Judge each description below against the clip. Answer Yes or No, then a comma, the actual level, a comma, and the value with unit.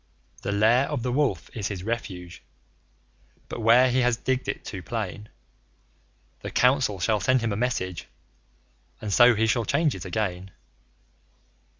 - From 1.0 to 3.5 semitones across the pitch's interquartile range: No, average, 3.9 semitones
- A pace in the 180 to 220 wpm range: No, average, 155 wpm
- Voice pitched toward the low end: Yes, low, 115 Hz